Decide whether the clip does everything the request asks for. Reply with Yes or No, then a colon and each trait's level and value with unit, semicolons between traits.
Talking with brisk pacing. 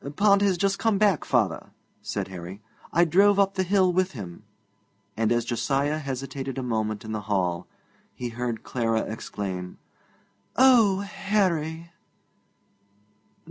No: slow, 135 wpm